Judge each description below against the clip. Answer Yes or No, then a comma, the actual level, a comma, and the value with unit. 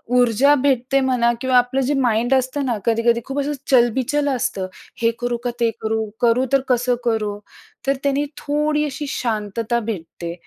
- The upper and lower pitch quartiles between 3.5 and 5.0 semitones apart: No, average, 2.8 semitones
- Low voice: No, high, 245 Hz